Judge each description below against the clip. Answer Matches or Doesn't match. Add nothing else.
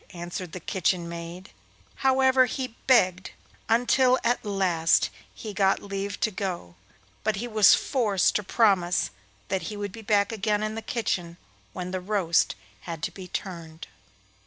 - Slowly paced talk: Doesn't match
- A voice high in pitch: Matches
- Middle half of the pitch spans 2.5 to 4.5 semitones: Matches